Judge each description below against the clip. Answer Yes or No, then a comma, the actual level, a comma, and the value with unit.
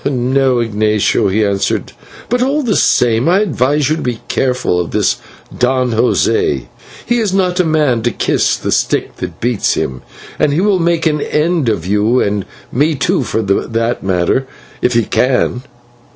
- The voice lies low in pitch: Yes, low, 125 Hz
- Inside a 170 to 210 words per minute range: Yes, average, 180 wpm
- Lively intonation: Yes, wide, 6.3 semitones